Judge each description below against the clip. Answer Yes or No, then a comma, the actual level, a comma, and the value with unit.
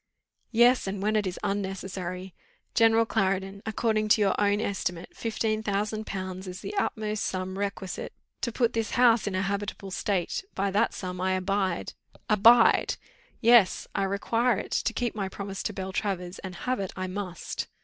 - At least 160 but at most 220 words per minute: Yes, average, 170 wpm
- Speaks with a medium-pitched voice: No, high, 200 Hz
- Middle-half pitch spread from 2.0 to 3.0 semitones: Yes, narrow, 2.6 semitones